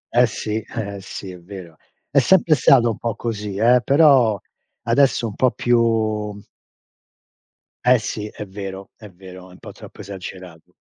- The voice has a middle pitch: No, low, 105 Hz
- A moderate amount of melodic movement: Yes, average, 3.6 semitones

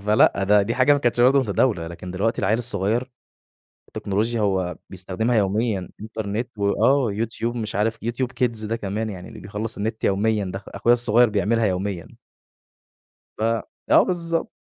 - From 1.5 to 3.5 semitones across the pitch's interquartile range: Yes, average, 3.0 semitones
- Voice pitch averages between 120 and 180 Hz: No, low, 110 Hz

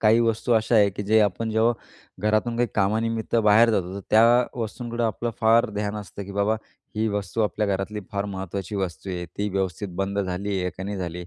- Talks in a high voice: No, low, 105 Hz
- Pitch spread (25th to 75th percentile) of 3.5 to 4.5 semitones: No, narrow, 2.5 semitones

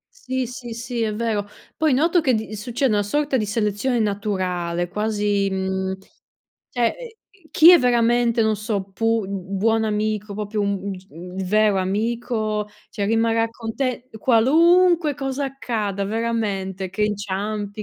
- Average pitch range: Yes, average, 3.1 semitones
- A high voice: Yes, high, 215 Hz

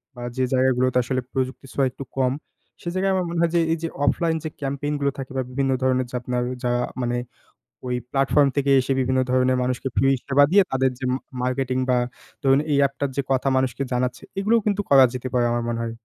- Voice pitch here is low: Yes, low, 130 Hz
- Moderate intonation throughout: No, narrow, 1.8 semitones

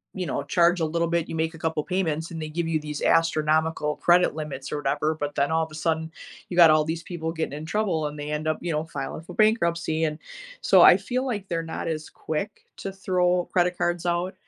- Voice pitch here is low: No, medium, 160 Hz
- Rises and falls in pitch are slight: Yes, narrow, 2.1 semitones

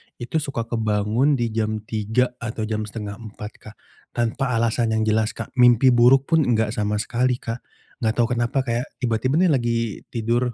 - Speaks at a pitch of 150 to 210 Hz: No, low, 115 Hz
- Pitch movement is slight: Yes, narrow, 2.1 semitones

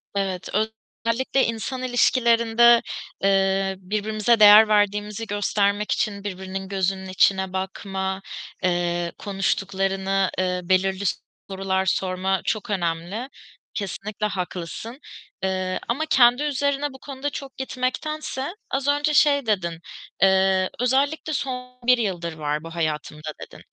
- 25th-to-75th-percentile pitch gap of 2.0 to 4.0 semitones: No, average, 4.5 semitones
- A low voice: No, high, 200 Hz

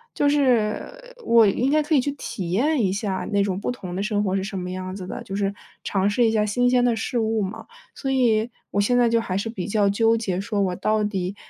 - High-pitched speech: Yes, high, 215 Hz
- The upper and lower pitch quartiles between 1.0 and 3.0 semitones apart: No, average, 3.9 semitones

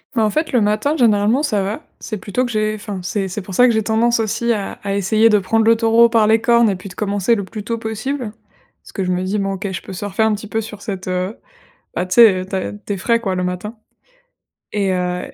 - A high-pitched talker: Yes, high, 210 Hz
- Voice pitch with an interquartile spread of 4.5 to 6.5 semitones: No, average, 2.8 semitones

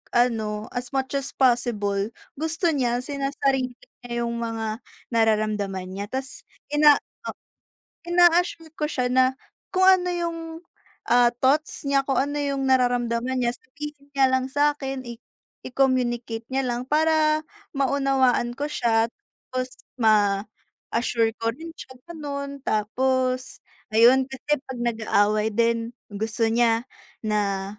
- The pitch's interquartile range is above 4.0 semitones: No, average, 3.5 semitones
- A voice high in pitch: Yes, very high, 255 Hz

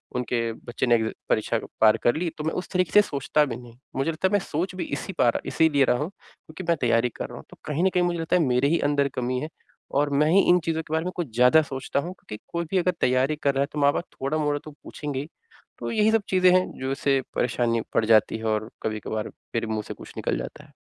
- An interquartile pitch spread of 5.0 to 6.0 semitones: Yes, wide, 5.6 semitones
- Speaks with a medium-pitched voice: Yes, medium, 145 Hz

